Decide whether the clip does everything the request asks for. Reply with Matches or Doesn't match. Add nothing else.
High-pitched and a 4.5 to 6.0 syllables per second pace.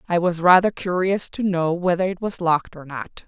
Doesn't match